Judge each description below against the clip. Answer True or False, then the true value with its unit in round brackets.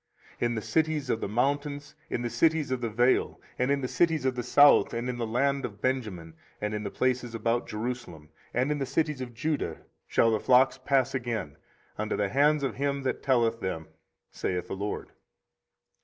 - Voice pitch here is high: False (125 Hz)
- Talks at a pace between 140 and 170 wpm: False (200 wpm)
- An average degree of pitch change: True (3.8 semitones)